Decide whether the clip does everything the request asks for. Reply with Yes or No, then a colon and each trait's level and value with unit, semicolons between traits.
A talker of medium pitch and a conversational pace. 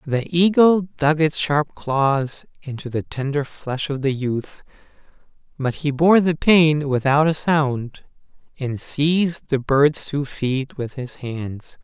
Yes: medium, 145 Hz; average, 150 wpm